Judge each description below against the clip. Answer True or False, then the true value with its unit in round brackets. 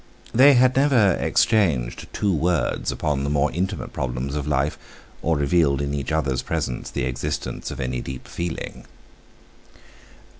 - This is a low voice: True (75 Hz)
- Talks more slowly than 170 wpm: True (145 wpm)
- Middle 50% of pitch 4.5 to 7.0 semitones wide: True (4.8 semitones)